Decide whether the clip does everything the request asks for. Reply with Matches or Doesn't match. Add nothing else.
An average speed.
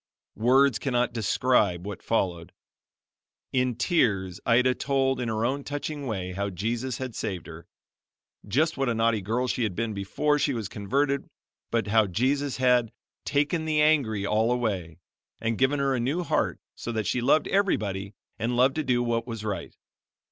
Matches